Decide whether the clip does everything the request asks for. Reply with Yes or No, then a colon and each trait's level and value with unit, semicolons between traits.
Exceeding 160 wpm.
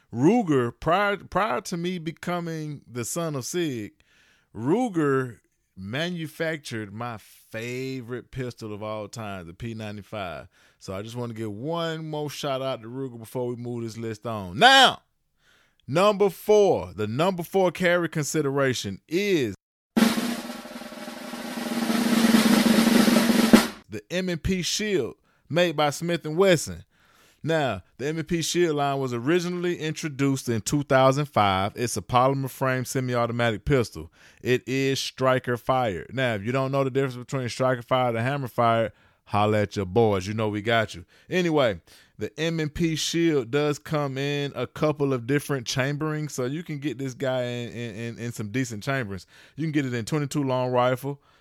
No: average, 145 wpm